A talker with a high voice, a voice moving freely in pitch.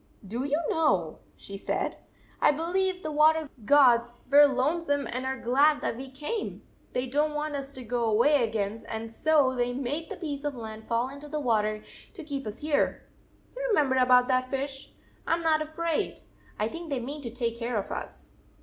No: very high, 270 Hz; average, 4.2 semitones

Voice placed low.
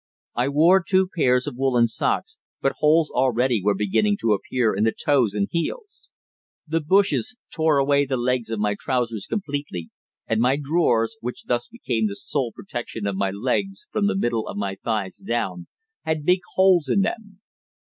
Yes: low, 130 Hz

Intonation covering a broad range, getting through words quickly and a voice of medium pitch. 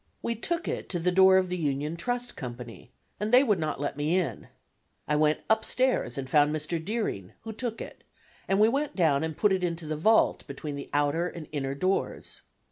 Yes: wide, 6.3 semitones; fast, 210 wpm; medium, 170 Hz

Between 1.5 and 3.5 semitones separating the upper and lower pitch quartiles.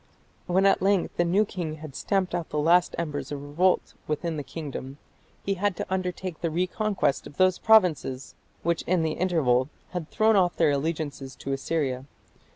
No: average, 4.2 semitones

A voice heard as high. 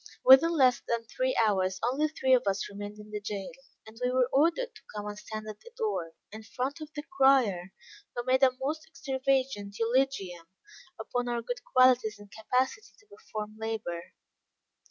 Yes: high, 245 Hz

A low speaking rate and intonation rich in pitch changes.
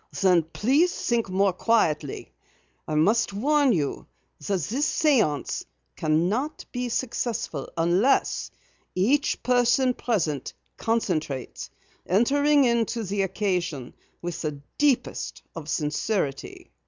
Yes: slow, 105 wpm; wide, 7.3 semitones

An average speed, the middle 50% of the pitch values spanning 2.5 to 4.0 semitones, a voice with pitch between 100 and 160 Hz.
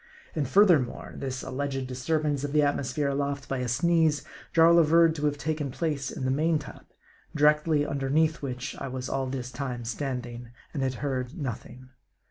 Yes: average, 170 wpm; average, 2.9 semitones; medium, 140 Hz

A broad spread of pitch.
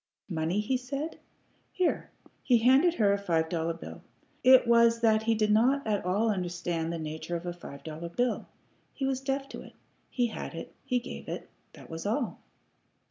Yes: wide, 6.6 semitones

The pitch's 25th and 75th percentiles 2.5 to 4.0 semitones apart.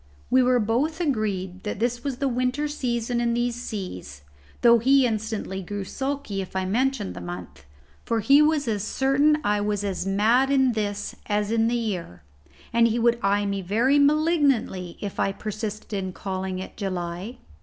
No: average, 4.6 semitones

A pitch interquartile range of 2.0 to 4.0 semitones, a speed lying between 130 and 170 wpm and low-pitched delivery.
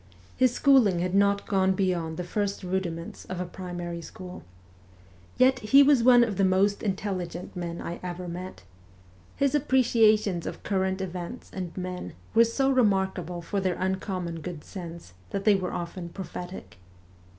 No: average, 2.8 semitones; average, 155 wpm; high, 190 Hz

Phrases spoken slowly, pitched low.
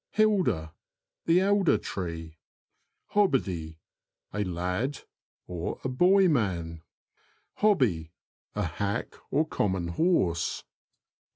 Yes: slow, 100 wpm; low, 100 Hz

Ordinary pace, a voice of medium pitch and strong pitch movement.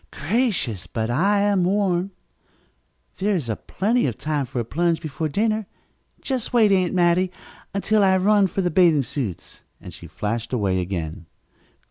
Yes: average, 155 wpm; medium, 175 Hz; wide, 8.2 semitones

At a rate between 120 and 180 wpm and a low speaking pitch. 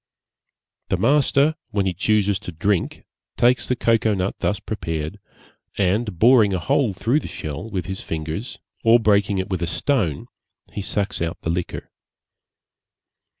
Yes: average, 150 wpm; low, 100 Hz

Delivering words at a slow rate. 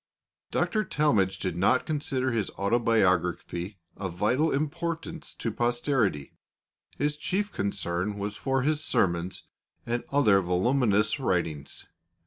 Yes: slow, 115 wpm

